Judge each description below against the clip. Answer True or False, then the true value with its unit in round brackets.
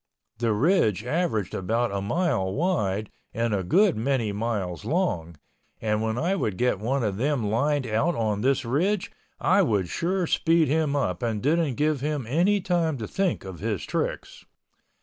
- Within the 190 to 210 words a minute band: False (170 wpm)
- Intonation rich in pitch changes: True (7.3 semitones)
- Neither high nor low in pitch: False (125 Hz)